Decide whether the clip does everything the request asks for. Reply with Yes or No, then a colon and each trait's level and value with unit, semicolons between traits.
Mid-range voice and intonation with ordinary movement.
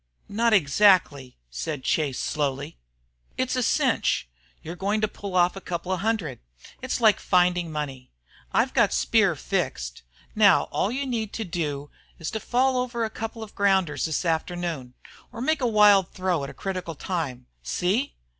No: medium, 180 Hz; wide, 6.4 semitones